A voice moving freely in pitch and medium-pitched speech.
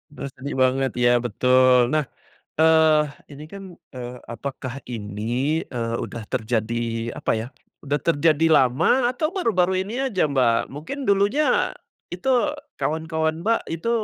Yes: wide, 6.2 semitones; medium, 145 Hz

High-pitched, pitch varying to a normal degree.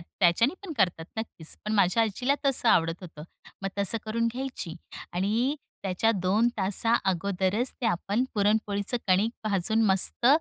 Yes: high, 205 Hz; average, 3.7 semitones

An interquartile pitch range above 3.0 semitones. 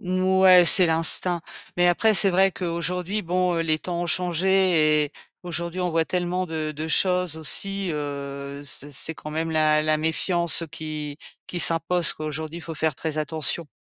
No: average, 2.7 semitones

